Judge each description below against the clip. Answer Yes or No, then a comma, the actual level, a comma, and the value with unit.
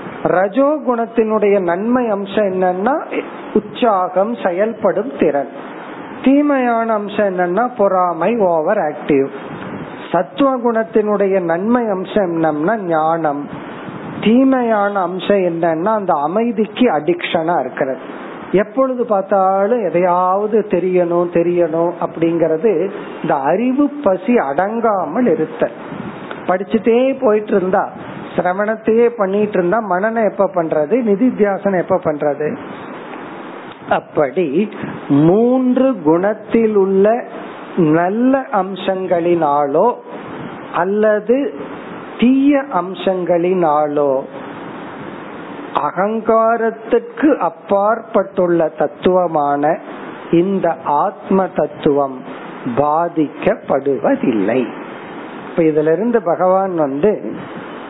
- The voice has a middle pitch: No, high, 195 Hz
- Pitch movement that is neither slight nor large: Yes, average, 4.9 semitones